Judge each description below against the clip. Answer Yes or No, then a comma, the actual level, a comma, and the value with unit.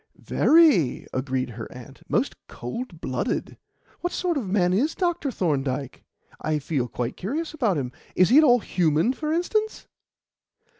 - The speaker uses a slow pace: No, average, 150 wpm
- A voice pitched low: No, medium, 185 Hz